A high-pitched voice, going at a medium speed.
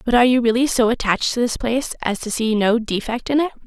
No: high, 235 Hz; fast, 260 wpm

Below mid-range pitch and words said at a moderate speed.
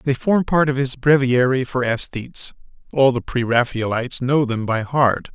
Yes: low, 130 Hz; average, 180 wpm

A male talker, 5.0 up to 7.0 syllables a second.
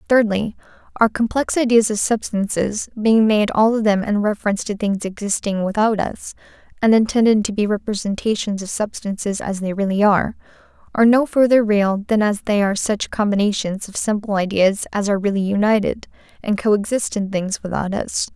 No: female; 5.4 syllables/s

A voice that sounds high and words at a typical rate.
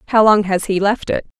No: high, 205 Hz; fast, 255 wpm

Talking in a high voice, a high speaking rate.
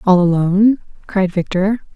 No: high, 195 Hz; slow, 125 wpm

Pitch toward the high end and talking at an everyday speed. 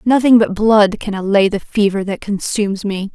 Yes: high, 205 Hz; average, 190 wpm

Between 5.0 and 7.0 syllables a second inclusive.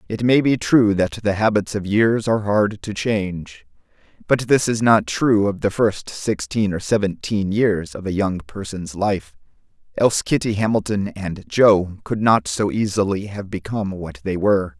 No: 4.5 syllables/s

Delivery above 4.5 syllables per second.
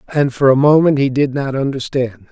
Yes: 5.5 syllables/s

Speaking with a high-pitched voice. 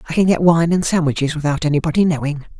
No: medium, 160 Hz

